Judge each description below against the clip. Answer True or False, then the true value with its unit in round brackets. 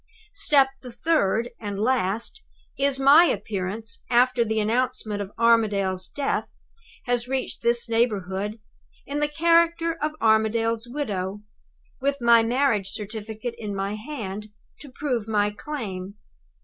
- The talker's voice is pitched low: False (230 Hz)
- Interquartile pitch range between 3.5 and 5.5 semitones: True (4.5 semitones)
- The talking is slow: True (125 wpm)